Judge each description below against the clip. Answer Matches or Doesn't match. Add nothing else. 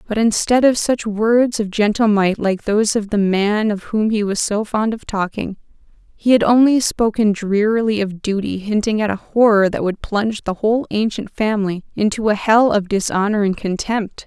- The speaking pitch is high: Matches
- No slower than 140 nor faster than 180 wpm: Doesn't match